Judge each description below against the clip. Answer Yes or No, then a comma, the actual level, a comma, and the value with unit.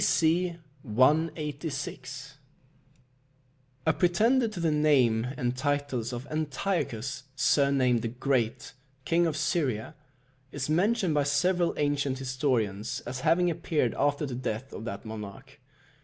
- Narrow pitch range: No, average, 4.3 semitones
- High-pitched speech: No, medium, 140 Hz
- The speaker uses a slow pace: Yes, slow, 120 wpm